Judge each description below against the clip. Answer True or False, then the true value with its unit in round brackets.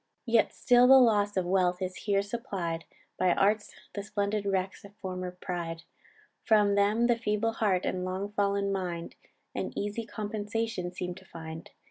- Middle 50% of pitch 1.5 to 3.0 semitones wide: True (2.6 semitones)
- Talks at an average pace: True (160 wpm)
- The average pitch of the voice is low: False (200 Hz)